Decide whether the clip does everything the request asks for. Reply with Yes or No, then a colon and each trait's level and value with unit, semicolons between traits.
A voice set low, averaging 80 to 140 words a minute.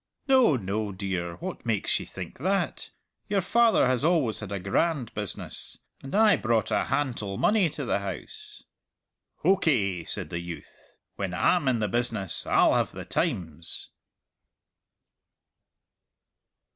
Yes: low, 120 Hz; slow, 135 wpm